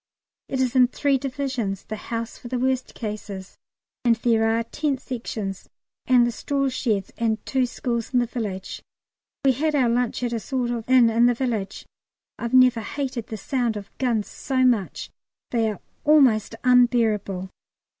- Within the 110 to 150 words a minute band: No, average, 175 wpm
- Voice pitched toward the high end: Yes, high, 240 Hz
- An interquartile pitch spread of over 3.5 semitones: No, average, 2.7 semitones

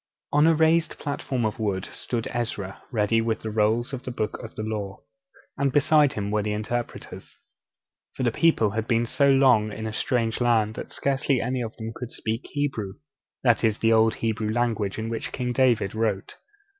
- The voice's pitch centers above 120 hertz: No, low, 115 Hz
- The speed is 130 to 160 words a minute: No, average, 195 wpm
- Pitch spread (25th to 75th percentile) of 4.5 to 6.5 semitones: No, average, 2.8 semitones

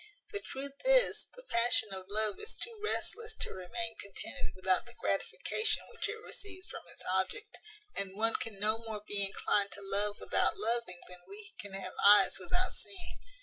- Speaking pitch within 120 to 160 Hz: No, high, 225 Hz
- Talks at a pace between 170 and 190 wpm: Yes, average, 180 wpm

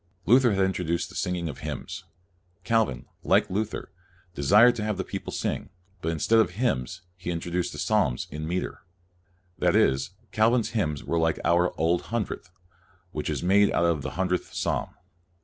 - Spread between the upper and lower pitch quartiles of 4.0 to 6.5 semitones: Yes, average, 4.3 semitones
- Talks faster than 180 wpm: No, average, 170 wpm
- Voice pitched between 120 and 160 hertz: No, very low, 90 Hz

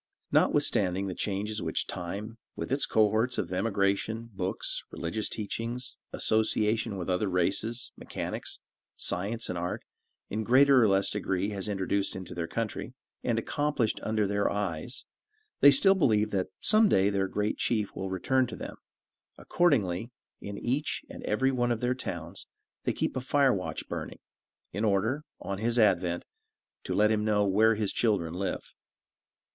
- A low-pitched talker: Yes, low, 105 Hz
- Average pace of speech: Yes, average, 160 wpm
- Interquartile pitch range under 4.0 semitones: Yes, average, 3.4 semitones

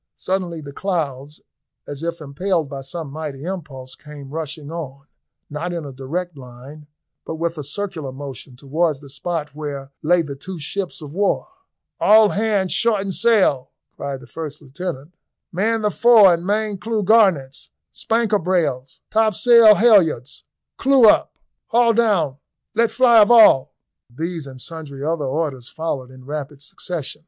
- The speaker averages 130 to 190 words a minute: Yes, average, 150 wpm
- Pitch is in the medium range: Yes, medium, 160 Hz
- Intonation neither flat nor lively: No, wide, 5.9 semitones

